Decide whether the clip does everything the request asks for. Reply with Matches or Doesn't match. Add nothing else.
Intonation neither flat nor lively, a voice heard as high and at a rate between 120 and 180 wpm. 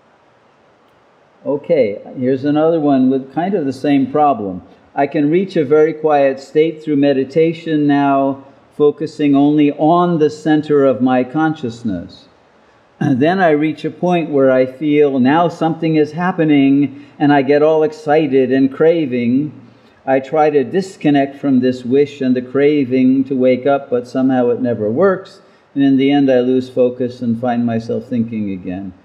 Doesn't match